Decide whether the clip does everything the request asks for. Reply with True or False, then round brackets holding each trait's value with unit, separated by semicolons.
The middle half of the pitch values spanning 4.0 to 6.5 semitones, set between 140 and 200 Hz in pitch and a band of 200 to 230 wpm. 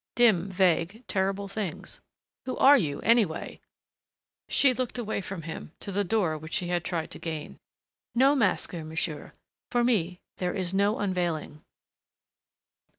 False (4.7 semitones; 190 Hz; 145 wpm)